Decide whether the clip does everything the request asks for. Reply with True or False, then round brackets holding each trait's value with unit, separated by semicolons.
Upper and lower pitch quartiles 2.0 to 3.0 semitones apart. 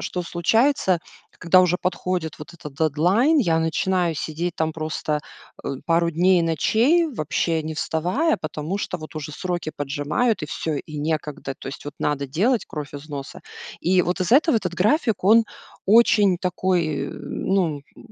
False (3.5 semitones)